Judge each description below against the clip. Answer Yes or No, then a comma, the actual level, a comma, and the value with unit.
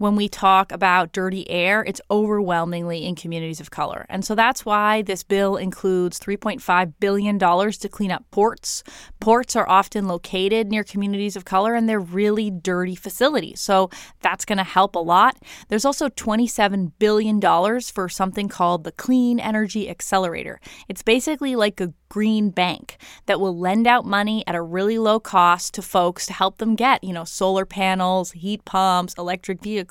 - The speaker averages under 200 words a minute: Yes, average, 175 wpm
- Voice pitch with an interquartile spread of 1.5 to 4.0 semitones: Yes, average, 2.7 semitones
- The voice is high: Yes, high, 200 Hz